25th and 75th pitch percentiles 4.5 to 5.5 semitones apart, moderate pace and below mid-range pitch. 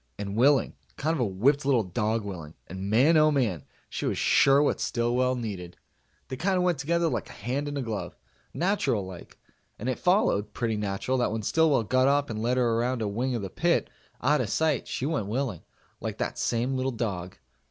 No: average, 4.9 semitones; fast, 210 wpm; low, 125 Hz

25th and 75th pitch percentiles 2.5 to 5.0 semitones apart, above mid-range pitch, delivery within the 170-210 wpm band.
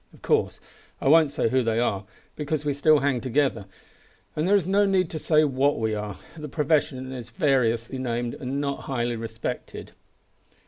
No: average, 4.4 semitones; low, 135 Hz; average, 180 wpm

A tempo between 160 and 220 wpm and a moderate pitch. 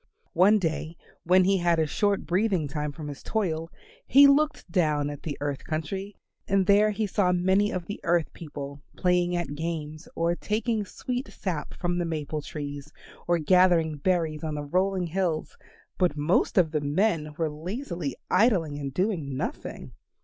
Yes: average, 170 wpm; medium, 170 Hz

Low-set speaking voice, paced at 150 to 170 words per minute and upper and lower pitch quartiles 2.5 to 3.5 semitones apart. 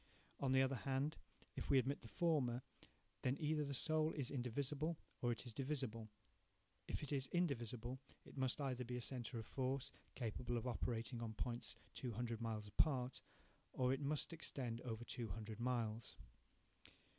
Yes: low, 125 Hz; average, 160 wpm; average, 2.9 semitones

